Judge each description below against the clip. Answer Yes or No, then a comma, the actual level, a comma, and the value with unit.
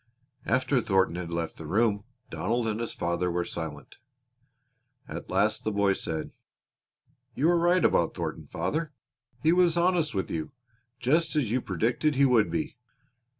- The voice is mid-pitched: No, low, 115 Hz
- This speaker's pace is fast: No, average, 155 wpm